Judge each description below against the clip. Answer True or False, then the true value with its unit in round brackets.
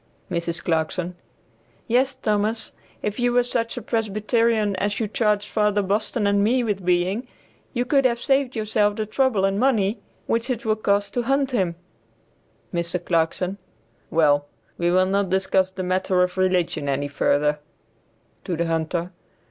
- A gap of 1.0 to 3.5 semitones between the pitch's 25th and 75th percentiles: False (4.2 semitones)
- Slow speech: False (155 wpm)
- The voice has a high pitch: True (200 Hz)